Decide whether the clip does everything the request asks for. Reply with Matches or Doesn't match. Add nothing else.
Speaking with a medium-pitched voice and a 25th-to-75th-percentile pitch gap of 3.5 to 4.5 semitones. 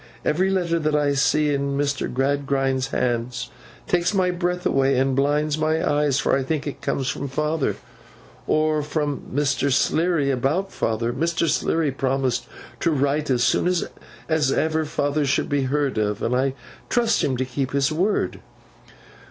Doesn't match